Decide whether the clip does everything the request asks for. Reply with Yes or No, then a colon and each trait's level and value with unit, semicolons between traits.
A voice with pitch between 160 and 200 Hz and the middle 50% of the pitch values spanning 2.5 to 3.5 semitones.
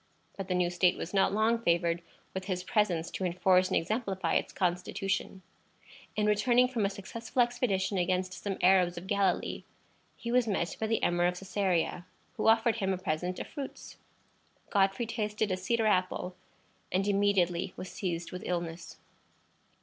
Yes: high, 190 Hz; average, 2.8 semitones